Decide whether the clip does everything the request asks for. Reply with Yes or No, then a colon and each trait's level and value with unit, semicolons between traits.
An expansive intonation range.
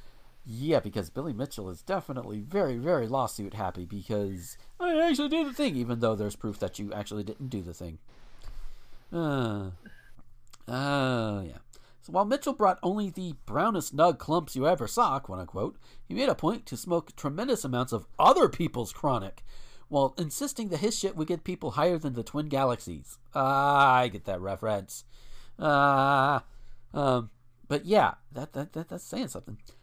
Yes: wide, 6.1 semitones